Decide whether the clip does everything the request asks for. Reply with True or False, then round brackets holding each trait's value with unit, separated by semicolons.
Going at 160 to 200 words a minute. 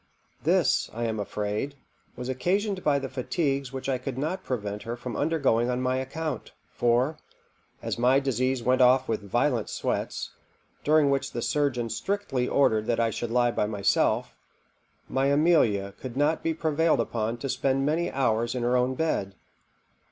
True (165 wpm)